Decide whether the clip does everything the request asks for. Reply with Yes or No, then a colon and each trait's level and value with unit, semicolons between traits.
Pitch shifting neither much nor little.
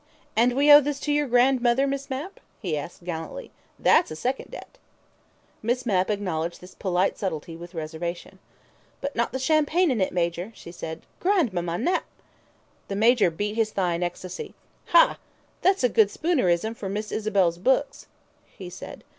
No: wide, 7.2 semitones